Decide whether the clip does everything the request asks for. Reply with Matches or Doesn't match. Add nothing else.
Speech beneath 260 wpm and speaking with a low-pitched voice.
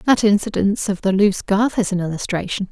Doesn't match